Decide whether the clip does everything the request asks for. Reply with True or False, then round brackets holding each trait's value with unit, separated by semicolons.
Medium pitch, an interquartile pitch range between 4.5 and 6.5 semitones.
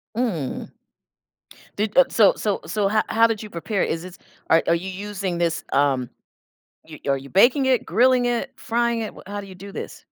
False (200 Hz; 5.1 semitones)